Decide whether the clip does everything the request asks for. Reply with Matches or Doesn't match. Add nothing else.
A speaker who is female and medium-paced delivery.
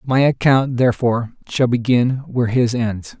Doesn't match